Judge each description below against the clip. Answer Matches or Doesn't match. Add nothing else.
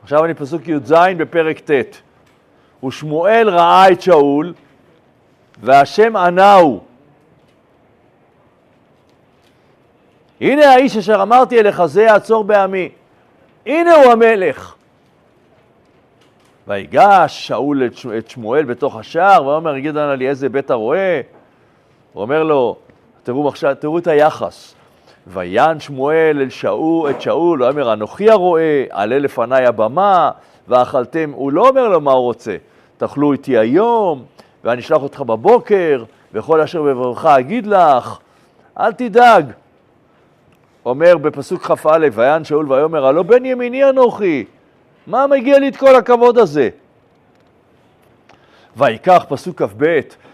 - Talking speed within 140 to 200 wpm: Doesn't match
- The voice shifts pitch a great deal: Matches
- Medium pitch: Matches